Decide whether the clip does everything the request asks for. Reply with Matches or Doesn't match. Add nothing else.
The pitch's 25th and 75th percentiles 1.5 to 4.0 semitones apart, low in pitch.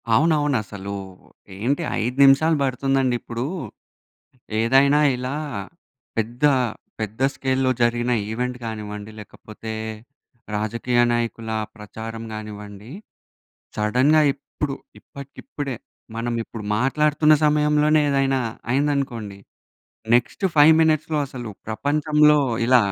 Doesn't match